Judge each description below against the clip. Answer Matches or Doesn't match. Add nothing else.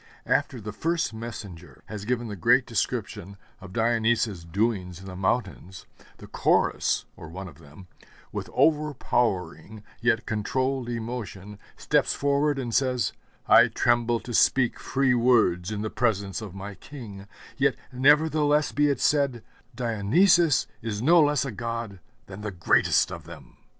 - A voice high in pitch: Doesn't match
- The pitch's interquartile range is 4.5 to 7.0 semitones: Matches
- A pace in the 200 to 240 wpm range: Doesn't match